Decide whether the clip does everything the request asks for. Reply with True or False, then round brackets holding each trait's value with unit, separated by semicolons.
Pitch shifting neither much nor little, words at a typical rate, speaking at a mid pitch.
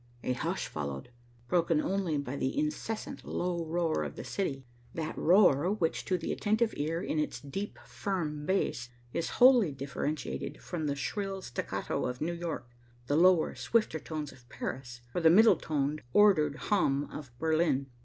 True (4.8 semitones; 165 wpm; 160 Hz)